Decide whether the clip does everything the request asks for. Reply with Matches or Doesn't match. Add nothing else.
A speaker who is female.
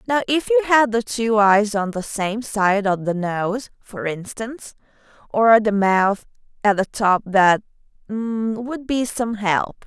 Matches